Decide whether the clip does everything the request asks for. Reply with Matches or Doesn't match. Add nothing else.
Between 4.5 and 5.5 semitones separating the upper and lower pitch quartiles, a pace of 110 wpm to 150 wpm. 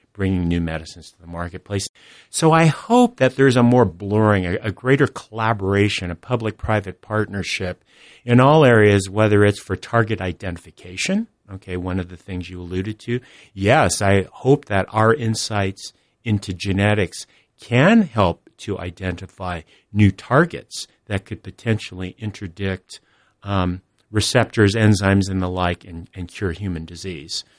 Doesn't match